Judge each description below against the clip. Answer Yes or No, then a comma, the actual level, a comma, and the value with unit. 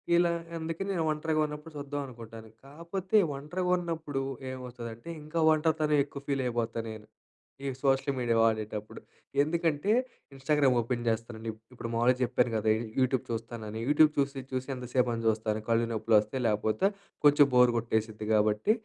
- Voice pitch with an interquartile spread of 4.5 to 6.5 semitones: Yes, average, 4.9 semitones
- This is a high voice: No, low, 125 Hz